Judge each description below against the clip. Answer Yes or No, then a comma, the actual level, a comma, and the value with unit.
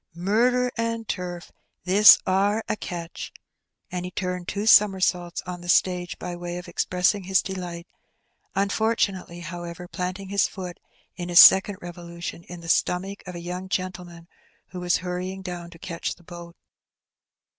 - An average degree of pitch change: No, narrow, 1.6 semitones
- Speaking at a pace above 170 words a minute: No, average, 155 wpm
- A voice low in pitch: No, medium, 180 Hz